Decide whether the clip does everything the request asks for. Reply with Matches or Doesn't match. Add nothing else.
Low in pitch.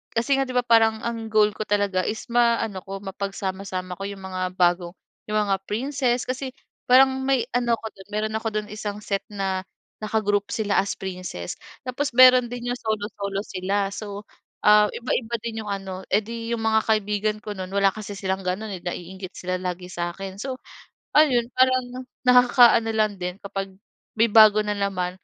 Doesn't match